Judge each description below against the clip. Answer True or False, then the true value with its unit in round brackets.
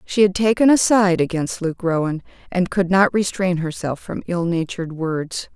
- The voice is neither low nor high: True (180 Hz)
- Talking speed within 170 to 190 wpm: True (185 wpm)